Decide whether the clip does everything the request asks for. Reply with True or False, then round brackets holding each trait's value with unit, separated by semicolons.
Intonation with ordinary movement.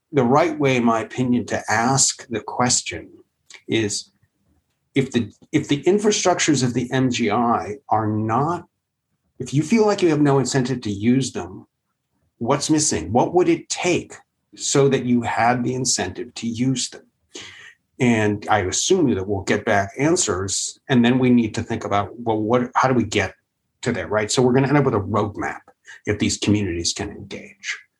True (4.2 semitones)